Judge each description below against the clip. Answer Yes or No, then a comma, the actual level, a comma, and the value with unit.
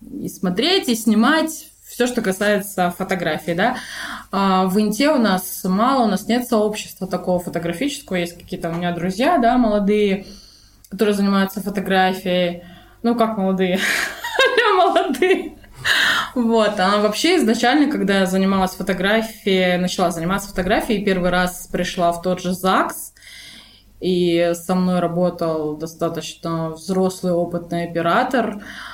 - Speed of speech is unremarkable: Yes, average, 125 wpm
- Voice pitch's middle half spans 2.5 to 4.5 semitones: Yes, average, 4.2 semitones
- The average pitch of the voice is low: No, high, 195 Hz